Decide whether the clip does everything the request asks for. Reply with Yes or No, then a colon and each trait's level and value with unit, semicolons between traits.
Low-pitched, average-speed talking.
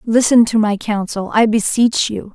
No: high, 220 Hz; average, 180 wpm